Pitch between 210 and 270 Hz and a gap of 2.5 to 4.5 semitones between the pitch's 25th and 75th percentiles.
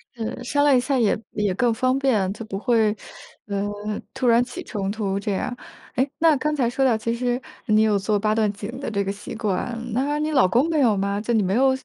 Yes: high, 230 Hz; average, 3.9 semitones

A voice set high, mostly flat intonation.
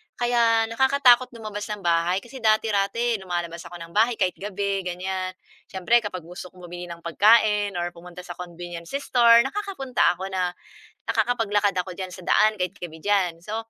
No: high, 195 Hz; average, 4.3 semitones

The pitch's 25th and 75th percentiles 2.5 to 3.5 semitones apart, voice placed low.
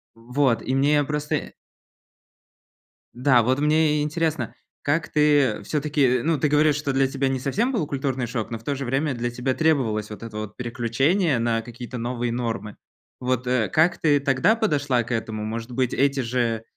No: average, 3.9 semitones; low, 130 Hz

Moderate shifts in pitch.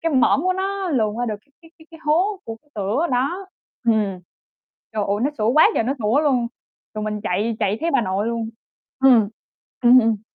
No: wide, 6.4 semitones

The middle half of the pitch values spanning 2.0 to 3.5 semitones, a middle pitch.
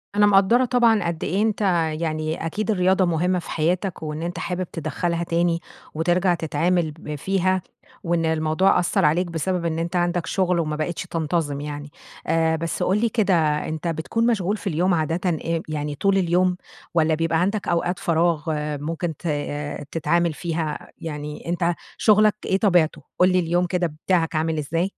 Yes: narrow, 2.4 semitones; medium, 170 Hz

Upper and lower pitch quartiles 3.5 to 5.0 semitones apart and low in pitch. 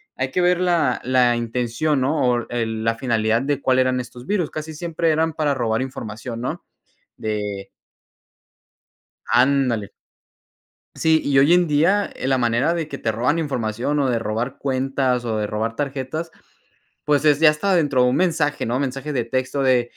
Yes: average, 4.2 semitones; low, 130 Hz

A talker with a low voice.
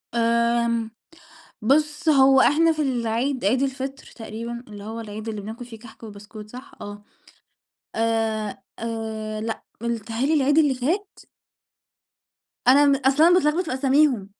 No: high, 235 Hz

